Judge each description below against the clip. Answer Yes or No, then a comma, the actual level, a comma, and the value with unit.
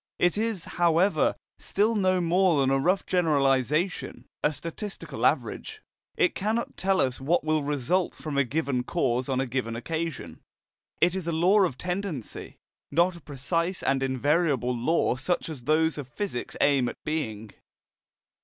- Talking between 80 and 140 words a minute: No, average, 155 wpm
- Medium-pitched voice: Yes, medium, 160 Hz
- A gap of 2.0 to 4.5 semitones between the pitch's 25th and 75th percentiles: No, average, 5.2 semitones